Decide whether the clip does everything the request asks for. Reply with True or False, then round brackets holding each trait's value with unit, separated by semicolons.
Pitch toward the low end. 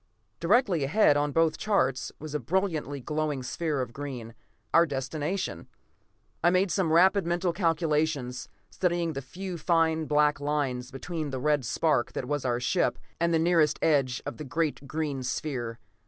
False (150 Hz)